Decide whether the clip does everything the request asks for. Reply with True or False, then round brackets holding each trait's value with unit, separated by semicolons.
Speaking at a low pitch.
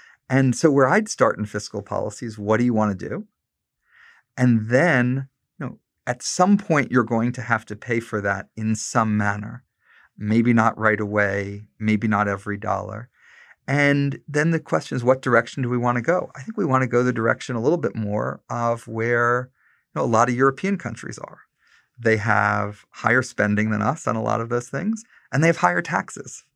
True (120 Hz)